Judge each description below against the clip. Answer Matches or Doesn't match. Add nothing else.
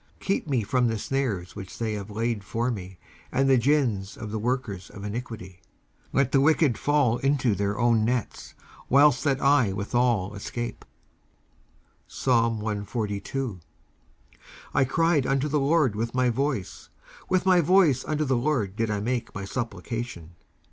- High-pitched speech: Doesn't match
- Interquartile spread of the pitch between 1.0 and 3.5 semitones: Doesn't match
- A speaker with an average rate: Matches